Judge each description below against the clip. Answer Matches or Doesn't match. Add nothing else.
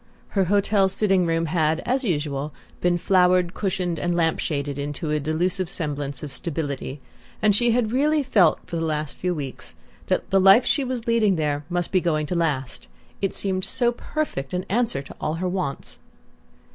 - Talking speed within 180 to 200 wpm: Matches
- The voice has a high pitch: Doesn't match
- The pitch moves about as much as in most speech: Matches